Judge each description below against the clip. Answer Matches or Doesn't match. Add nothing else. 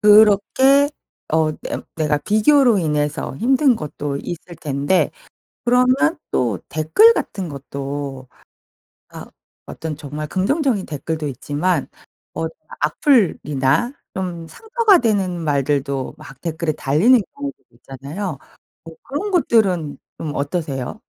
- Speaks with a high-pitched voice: Doesn't match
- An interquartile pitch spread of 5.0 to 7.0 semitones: Doesn't match